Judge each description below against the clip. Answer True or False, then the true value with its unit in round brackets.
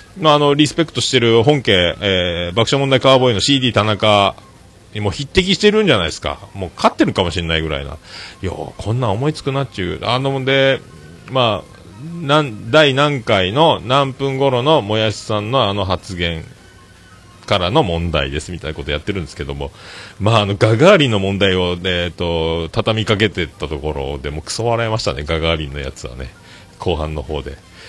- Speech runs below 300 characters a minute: False (375 characters per minute)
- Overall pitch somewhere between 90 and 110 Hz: True (100 Hz)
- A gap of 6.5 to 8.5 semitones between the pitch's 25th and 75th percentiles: True (7.1 semitones)